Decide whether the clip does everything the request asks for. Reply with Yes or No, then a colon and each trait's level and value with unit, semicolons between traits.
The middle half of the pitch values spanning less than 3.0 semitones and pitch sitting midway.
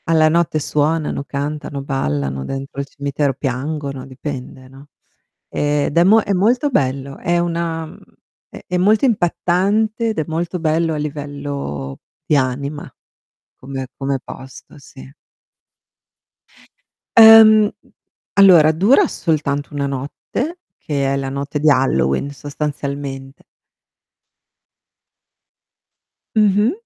No: average, 4.0 semitones; medium, 145 Hz